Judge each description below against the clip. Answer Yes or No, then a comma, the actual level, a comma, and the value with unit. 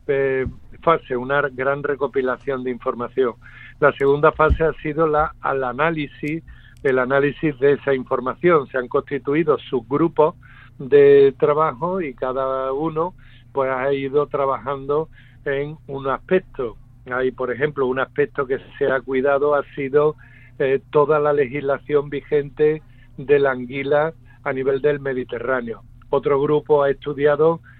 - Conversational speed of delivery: Yes, average, 135 wpm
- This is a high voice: No, medium, 140 Hz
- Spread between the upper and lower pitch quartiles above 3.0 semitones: No, narrow, 2.4 semitones